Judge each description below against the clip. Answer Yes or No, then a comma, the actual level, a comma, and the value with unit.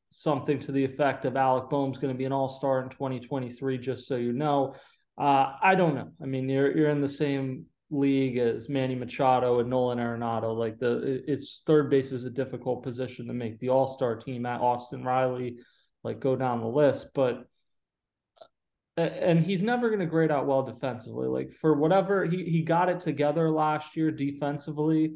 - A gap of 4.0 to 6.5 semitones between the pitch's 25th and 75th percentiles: No, average, 2.9 semitones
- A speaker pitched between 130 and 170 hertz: Yes, low, 135 Hz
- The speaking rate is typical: Yes, average, 190 wpm